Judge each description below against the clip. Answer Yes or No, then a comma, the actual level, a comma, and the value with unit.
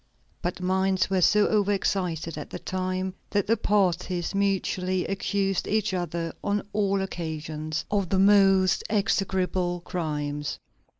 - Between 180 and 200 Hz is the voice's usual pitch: Yes, medium, 185 Hz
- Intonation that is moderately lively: No, narrow, 2.2 semitones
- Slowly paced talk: Yes, slow, 125 wpm